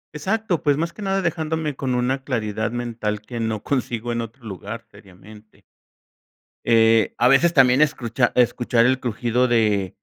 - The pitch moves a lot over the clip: No, average, 3.6 semitones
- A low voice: Yes, low, 120 Hz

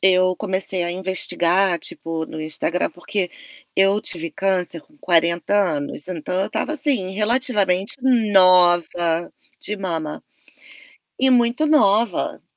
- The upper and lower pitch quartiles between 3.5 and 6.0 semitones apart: No, average, 2.9 semitones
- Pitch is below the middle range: No, medium, 185 Hz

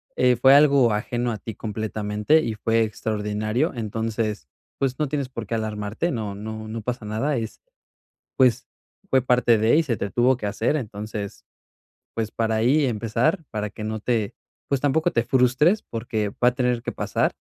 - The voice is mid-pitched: No, low, 115 Hz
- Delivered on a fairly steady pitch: No, average, 3.1 semitones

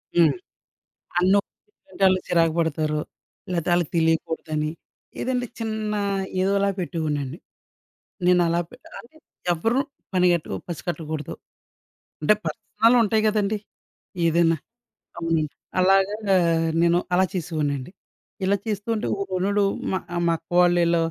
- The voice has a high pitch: No, medium, 180 Hz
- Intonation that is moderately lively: Yes, average, 3.7 semitones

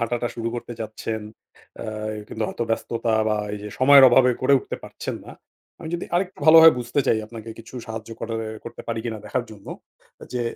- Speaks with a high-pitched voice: No, low, 115 Hz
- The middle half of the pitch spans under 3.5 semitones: Yes, narrow, 2.5 semitones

